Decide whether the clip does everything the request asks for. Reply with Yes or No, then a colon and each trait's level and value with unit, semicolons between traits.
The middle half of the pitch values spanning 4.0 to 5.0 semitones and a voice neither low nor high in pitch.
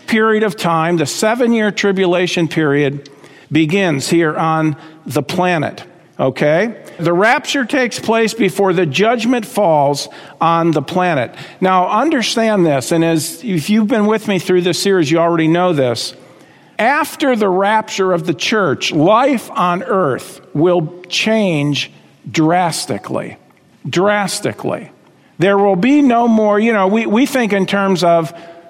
Yes: average, 4.7 semitones; medium, 180 Hz